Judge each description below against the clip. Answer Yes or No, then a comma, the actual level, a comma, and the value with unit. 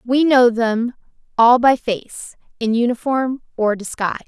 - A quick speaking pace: No, average, 140 wpm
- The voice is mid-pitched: No, high, 240 Hz